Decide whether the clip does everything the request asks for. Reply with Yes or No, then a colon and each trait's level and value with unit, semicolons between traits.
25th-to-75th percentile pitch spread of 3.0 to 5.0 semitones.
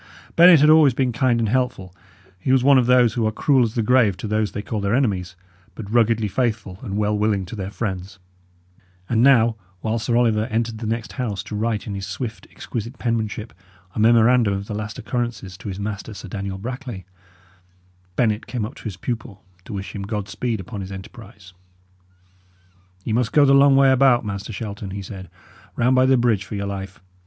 Yes: average, 3.3 semitones